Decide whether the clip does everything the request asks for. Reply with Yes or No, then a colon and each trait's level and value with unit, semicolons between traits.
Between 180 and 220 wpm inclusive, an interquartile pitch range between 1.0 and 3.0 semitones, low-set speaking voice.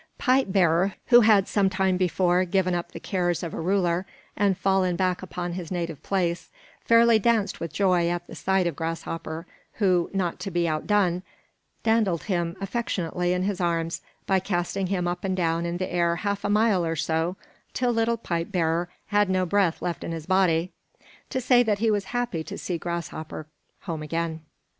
No: average, 185 wpm; average, 2.7 semitones; medium, 180 Hz